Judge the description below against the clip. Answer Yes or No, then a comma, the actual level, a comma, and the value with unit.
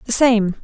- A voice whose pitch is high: Yes, high, 225 Hz